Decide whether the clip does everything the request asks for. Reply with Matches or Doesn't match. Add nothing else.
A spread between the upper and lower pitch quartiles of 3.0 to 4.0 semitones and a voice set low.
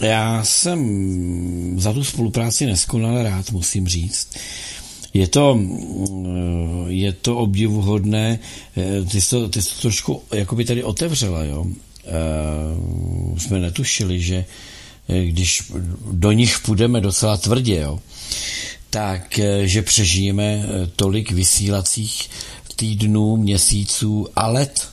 Matches